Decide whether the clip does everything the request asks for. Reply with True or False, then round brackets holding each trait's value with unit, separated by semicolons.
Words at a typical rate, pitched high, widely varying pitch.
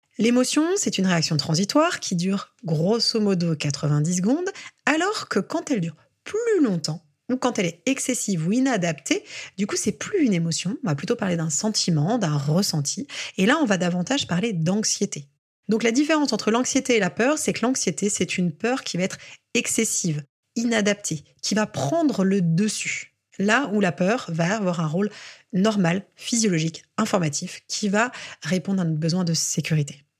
True (175 wpm; 195 Hz; 5.9 semitones)